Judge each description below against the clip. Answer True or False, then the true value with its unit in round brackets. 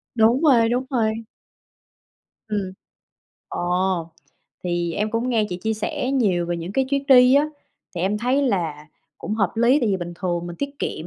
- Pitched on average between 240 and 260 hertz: False (215 Hz)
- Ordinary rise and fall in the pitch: False (6.1 semitones)